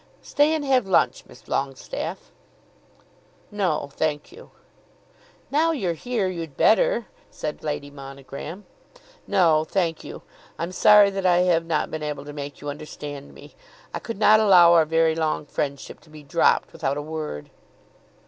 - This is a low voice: No, medium, 165 Hz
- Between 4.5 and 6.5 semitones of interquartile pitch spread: Yes, average, 5.0 semitones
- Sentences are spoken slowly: No, average, 155 wpm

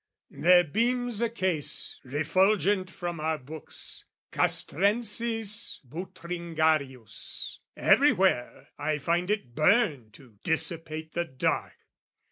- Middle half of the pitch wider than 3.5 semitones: Yes, average, 4.9 semitones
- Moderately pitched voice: Yes, medium, 170 Hz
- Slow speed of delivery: Yes, slow, 95 wpm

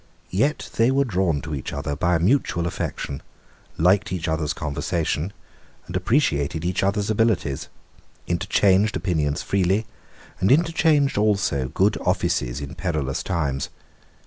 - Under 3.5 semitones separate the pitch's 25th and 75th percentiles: No, average, 5.2 semitones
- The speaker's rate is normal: No, slow, 125 wpm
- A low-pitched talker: Yes, very low, 90 Hz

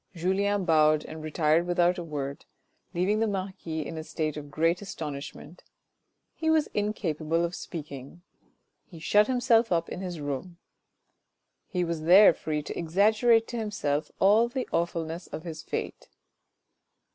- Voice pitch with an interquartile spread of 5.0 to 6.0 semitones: No, average, 4.4 semitones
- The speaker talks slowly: No, average, 145 wpm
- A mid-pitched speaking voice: Yes, medium, 170 Hz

